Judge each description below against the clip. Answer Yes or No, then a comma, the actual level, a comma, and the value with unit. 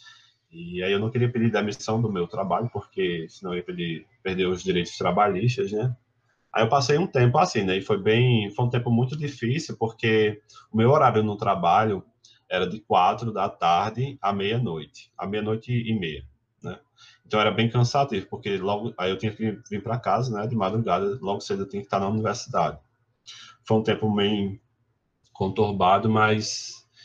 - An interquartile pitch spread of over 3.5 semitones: No, average, 3.2 semitones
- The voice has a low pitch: Yes, low, 110 Hz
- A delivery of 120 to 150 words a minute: No, average, 180 wpm